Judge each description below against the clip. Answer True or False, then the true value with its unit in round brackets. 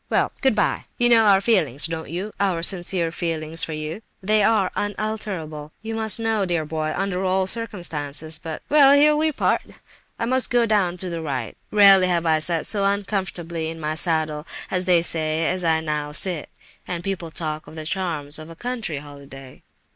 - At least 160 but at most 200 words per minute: True (175 wpm)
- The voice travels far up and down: False (4.6 semitones)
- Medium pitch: True (175 Hz)